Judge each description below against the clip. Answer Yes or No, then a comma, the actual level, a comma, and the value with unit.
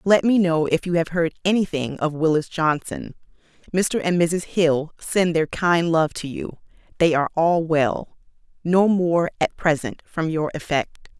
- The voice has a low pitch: No, medium, 165 Hz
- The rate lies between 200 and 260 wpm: No, average, 170 wpm